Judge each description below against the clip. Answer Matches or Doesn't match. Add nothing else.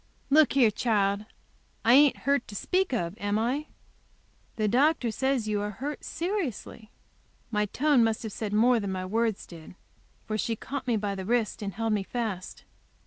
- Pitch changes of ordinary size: Matches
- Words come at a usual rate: Matches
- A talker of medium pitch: Doesn't match